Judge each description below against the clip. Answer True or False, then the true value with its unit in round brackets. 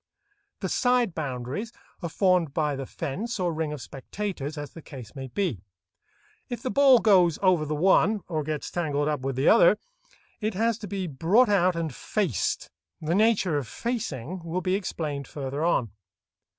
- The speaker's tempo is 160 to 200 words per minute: True (175 wpm)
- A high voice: False (170 Hz)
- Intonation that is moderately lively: False (5.8 semitones)